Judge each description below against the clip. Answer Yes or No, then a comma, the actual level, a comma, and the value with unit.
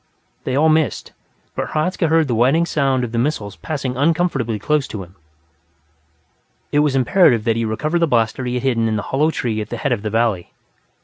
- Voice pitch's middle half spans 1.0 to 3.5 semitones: No, average, 5.2 semitones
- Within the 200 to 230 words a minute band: Yes, fast, 205 wpm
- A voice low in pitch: Yes, low, 130 Hz